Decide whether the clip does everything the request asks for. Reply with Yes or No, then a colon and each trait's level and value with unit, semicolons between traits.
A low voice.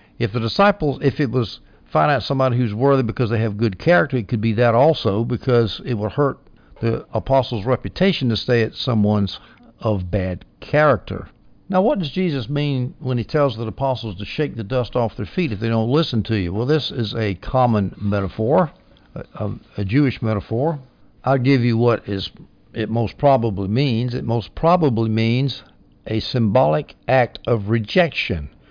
Yes: low, 120 Hz